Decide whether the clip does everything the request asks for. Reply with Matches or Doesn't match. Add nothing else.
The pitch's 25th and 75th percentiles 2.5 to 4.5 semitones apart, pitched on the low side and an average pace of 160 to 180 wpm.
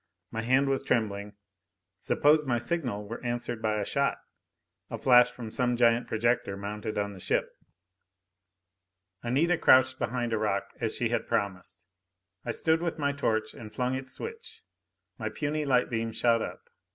Matches